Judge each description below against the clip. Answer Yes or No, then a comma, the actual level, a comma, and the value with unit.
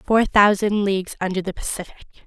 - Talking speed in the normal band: Yes, average, 160 wpm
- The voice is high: Yes, high, 195 Hz